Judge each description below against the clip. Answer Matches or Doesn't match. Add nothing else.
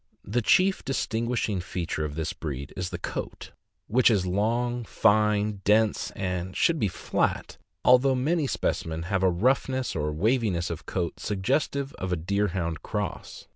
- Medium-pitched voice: Doesn't match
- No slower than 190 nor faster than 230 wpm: Doesn't match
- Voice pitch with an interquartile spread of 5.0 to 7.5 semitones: Matches